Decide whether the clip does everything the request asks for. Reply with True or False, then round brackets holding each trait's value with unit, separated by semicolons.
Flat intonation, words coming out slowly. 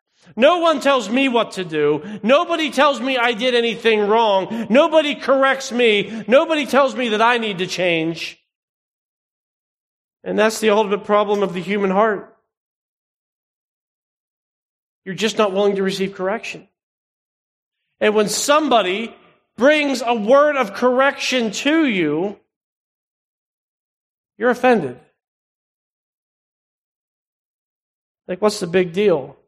False (5.1 semitones; 120 wpm)